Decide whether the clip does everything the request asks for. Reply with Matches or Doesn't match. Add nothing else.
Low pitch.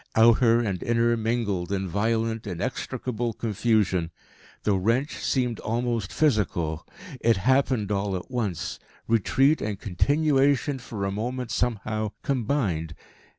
Matches